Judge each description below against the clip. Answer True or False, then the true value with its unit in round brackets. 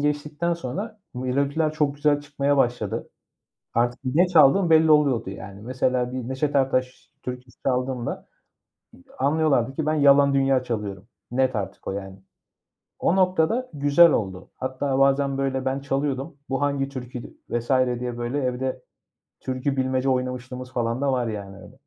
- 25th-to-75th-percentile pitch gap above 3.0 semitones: False (2.5 semitones)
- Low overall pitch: True (130 Hz)